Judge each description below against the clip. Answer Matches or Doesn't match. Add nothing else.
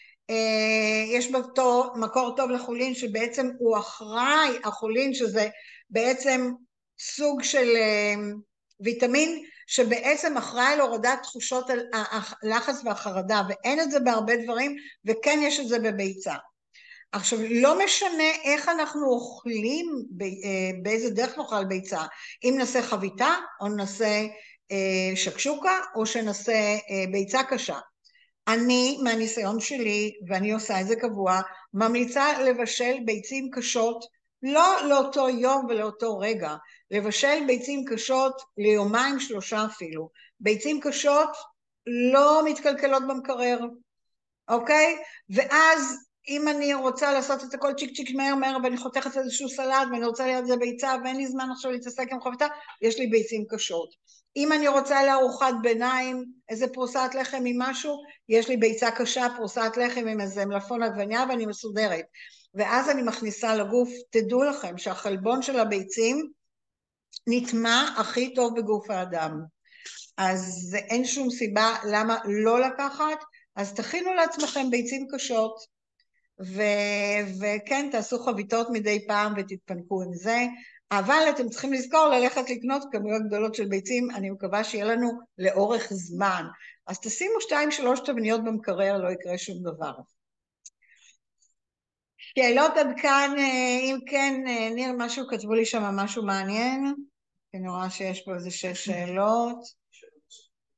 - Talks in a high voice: Matches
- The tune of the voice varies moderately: Matches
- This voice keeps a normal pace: Matches